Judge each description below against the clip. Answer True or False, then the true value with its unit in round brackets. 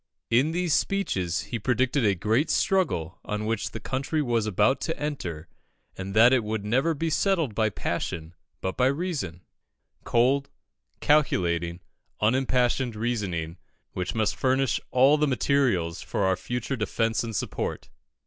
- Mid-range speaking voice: False (120 Hz)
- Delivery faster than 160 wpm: False (145 wpm)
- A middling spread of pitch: False (5.8 semitones)